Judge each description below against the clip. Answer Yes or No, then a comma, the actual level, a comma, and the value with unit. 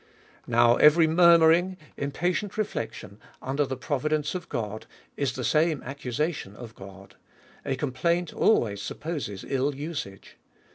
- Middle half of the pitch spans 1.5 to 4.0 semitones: No, wide, 5.6 semitones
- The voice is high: No, medium, 140 Hz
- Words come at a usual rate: No, slow, 125 wpm